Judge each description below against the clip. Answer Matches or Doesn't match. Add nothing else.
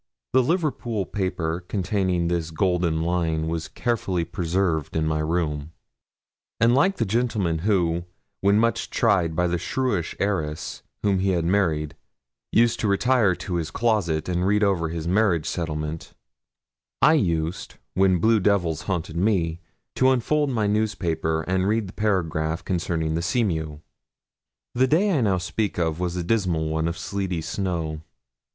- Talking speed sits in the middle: Matches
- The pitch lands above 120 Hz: Doesn't match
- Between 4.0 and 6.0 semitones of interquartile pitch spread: Matches